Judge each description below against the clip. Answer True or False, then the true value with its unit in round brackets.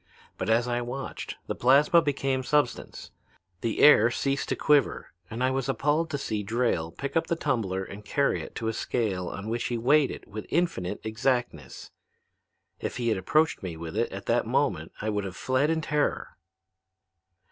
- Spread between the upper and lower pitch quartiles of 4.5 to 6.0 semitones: True (4.9 semitones)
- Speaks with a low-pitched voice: True (120 Hz)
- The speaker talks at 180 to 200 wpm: True (185 wpm)